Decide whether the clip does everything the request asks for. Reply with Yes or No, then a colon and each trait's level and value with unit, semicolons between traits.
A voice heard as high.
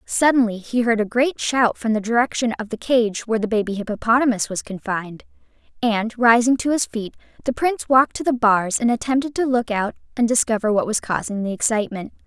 Yes: high, 230 Hz